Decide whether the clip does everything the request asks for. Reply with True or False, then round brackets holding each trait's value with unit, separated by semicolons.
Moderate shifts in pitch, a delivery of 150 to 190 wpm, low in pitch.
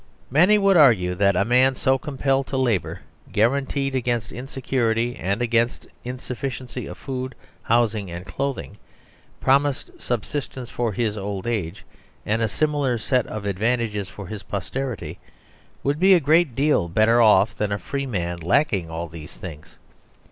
True (4.9 semitones; 155 wpm; 120 Hz)